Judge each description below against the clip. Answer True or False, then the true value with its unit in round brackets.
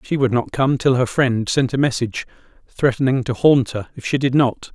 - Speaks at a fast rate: True (230 wpm)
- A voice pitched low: True (125 Hz)